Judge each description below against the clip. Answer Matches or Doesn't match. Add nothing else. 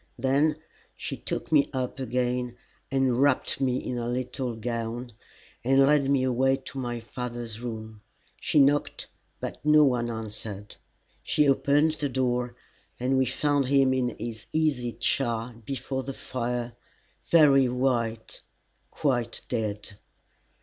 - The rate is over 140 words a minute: Doesn't match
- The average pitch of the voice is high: Doesn't match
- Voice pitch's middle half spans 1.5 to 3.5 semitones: Matches